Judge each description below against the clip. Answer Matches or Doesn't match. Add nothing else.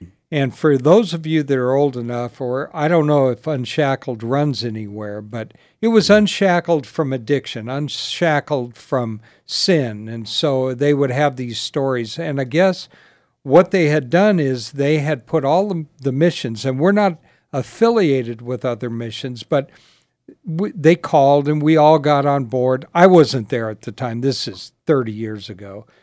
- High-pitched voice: Doesn't match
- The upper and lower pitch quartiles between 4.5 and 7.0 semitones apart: Matches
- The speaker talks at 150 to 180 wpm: Matches